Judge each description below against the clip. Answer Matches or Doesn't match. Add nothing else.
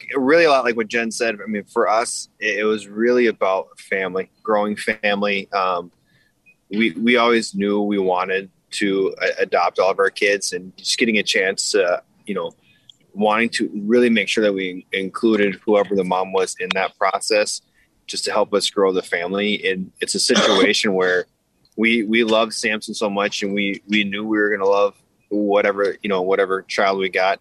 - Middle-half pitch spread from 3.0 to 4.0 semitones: Doesn't match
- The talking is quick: Doesn't match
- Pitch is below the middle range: Matches